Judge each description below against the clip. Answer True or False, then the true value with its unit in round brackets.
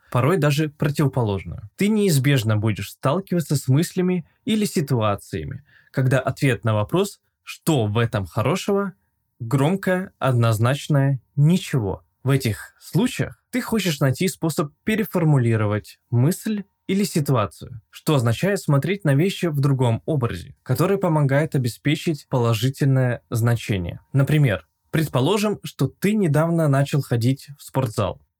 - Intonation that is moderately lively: False (6.6 semitones)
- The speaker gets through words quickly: False (115 wpm)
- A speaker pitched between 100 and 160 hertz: True (140 Hz)